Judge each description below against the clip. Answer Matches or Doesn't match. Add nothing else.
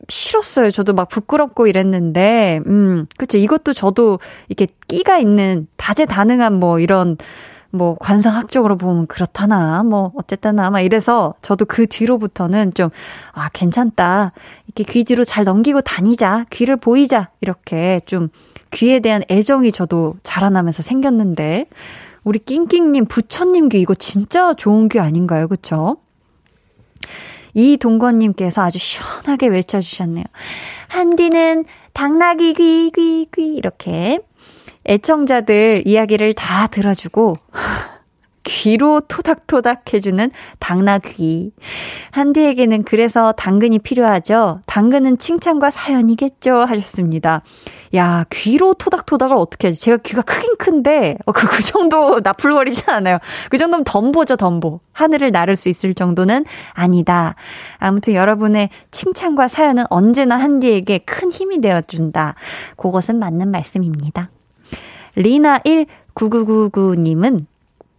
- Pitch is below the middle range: Doesn't match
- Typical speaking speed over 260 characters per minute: Matches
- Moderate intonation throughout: Doesn't match